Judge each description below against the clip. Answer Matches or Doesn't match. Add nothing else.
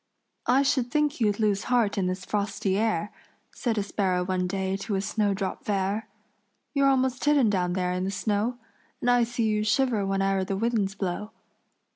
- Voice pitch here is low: Doesn't match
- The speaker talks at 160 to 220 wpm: Matches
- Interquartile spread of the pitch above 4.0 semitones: Doesn't match